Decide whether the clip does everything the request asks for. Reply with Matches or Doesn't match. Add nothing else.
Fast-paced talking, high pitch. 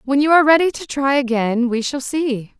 Matches